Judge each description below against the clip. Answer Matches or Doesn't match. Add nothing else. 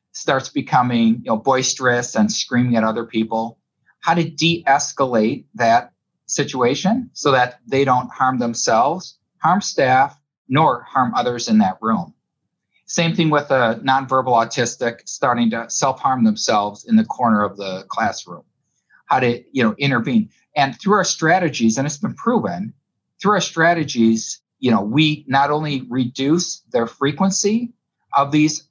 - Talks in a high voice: Doesn't match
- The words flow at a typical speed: Matches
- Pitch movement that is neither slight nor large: Doesn't match